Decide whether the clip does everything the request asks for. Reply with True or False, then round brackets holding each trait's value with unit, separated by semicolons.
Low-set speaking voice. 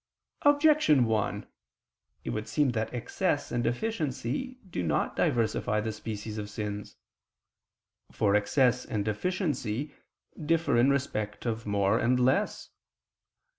True (120 Hz)